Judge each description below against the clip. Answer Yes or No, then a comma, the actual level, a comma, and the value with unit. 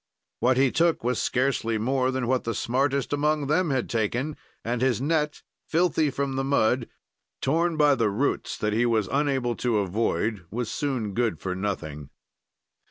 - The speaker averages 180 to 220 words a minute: No, average, 165 wpm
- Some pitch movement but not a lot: Yes, average, 4.0 semitones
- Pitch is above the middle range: No, low, 130 Hz